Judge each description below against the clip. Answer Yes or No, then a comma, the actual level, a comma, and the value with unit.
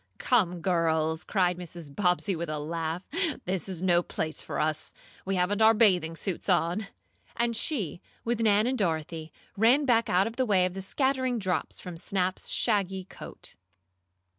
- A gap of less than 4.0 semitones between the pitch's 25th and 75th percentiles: No, average, 4.3 semitones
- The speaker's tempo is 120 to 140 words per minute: No, average, 165 wpm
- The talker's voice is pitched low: No, medium, 185 Hz